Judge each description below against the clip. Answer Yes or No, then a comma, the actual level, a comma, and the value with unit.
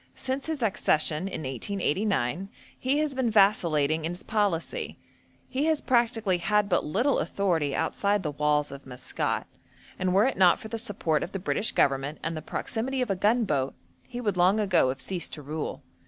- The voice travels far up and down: Yes, wide, 6.2 semitones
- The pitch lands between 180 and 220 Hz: Yes, high, 190 Hz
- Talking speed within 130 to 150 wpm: No, average, 185 wpm